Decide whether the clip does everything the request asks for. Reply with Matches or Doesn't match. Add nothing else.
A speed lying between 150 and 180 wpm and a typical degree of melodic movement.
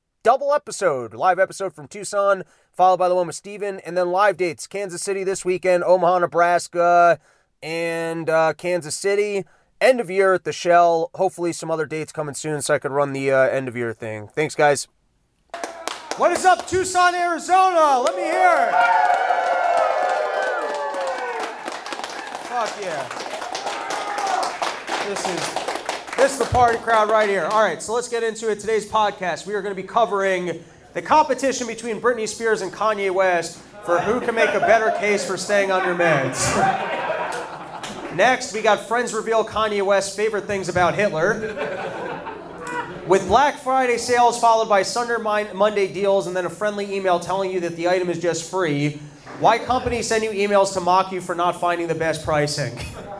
Matches